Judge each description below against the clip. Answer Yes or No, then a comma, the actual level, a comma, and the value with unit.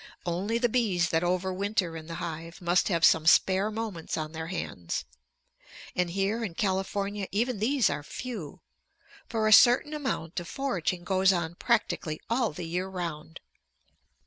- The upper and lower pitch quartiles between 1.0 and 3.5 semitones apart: No, average, 4.4 semitones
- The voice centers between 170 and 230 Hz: Yes, medium, 185 Hz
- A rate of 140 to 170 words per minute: Yes, average, 160 wpm